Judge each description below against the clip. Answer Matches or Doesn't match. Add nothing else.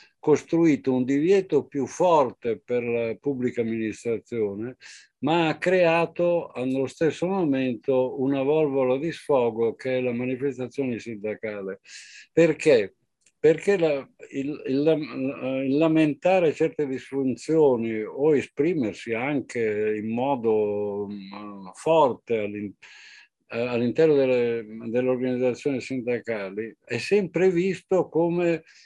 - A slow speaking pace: Matches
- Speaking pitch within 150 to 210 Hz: Doesn't match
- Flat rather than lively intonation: Doesn't match